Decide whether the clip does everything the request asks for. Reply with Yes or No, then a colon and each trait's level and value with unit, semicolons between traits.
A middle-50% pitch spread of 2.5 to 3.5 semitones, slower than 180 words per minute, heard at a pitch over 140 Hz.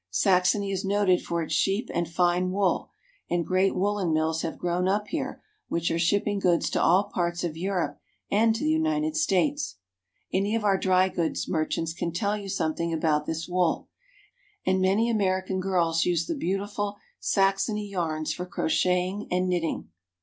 Yes: average, 2.9 semitones; average, 170 wpm; medium, 185 Hz